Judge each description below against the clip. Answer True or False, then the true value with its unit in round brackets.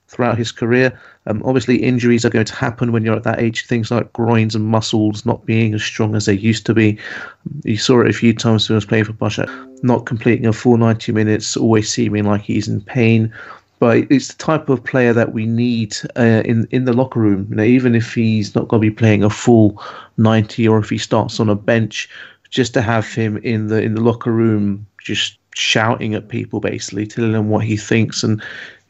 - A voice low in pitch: True (115 Hz)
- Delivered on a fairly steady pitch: True (1.6 semitones)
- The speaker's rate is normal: False (225 wpm)